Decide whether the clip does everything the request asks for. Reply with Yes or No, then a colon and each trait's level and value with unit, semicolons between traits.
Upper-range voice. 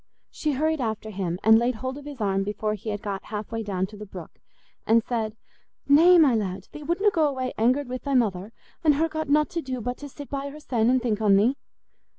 Yes: high, 245 Hz